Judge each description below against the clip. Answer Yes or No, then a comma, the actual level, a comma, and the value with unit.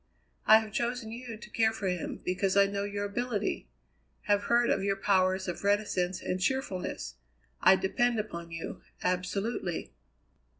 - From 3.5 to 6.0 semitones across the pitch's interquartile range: No, average, 3.0 semitones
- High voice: Yes, high, 200 Hz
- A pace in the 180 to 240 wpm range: No, average, 155 wpm